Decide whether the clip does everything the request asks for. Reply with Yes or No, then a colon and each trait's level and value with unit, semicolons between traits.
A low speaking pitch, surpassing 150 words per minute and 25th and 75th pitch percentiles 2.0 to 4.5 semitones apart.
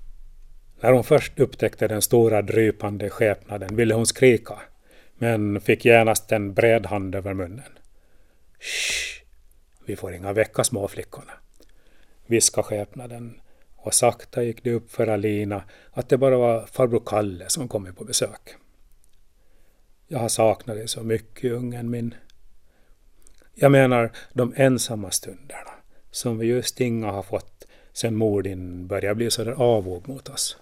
No: low, 115 Hz; average, 145 wpm; average, 2.9 semitones